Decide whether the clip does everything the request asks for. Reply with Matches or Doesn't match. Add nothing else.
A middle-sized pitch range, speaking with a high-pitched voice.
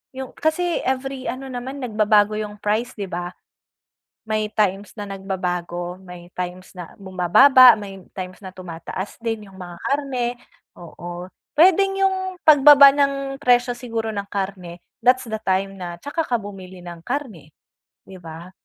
Doesn't match